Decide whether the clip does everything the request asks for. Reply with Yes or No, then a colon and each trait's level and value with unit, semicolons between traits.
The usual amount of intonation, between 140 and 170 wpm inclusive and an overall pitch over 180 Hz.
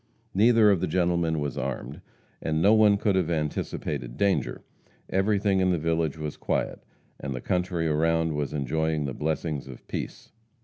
No: average, 3.8 semitones; average, 165 wpm; very low, 80 Hz